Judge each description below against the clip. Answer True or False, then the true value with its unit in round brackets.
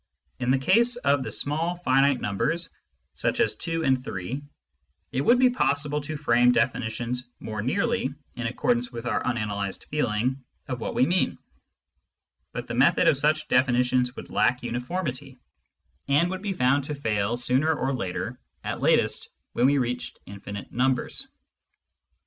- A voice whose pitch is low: True (130 Hz)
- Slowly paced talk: False (155 wpm)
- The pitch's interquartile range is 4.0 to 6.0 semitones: False (3.6 semitones)